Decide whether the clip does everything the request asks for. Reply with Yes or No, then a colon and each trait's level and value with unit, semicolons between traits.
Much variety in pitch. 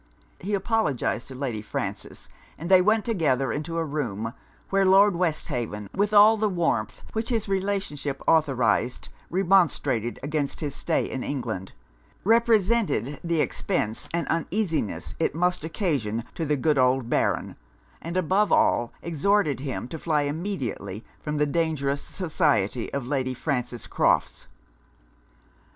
Yes: wide, 6.6 semitones